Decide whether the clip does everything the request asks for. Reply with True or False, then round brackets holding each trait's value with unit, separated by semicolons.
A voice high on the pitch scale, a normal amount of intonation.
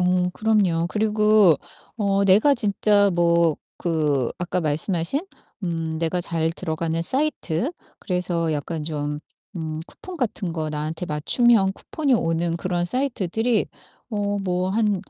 False (180 Hz; 4.3 semitones)